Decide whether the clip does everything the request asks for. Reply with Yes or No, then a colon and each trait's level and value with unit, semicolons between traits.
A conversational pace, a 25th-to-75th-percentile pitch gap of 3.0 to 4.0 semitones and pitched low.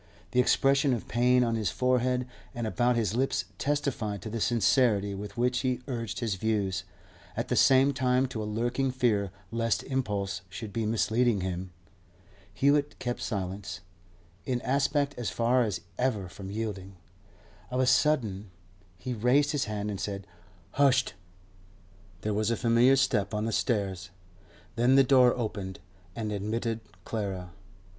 Yes: average, 150 wpm; average, 3.7 semitones; low, 115 Hz